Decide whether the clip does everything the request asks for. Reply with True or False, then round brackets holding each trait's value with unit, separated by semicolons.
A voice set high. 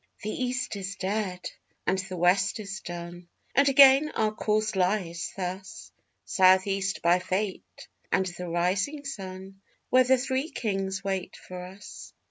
True (195 Hz)